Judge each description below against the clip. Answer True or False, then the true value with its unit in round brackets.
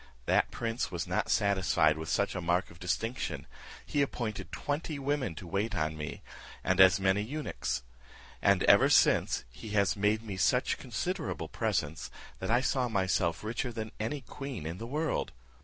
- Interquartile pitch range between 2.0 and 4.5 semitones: False (5.2 semitones)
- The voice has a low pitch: True (105 Hz)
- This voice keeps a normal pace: True (170 wpm)